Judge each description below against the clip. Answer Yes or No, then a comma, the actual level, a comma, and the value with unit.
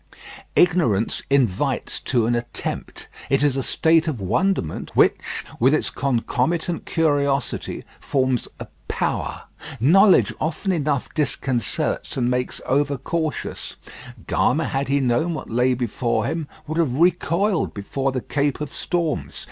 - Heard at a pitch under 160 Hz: Yes, medium, 140 Hz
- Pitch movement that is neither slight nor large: Yes, average, 4.5 semitones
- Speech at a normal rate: No, slow, 130 wpm